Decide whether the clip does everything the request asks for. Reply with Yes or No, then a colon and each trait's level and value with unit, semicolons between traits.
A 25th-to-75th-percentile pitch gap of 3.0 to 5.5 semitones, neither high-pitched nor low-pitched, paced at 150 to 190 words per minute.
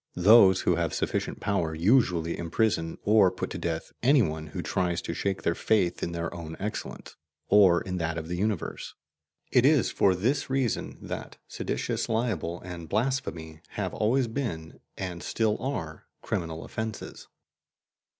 No: average, 4.9 semitones; very low, 95 Hz; average, 155 wpm